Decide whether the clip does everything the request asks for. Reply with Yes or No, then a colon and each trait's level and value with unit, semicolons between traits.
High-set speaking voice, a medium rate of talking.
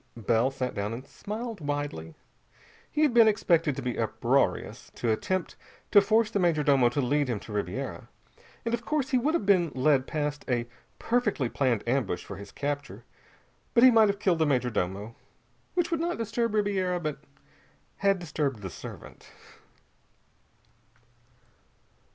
No: medium, 150 Hz; average, 160 wpm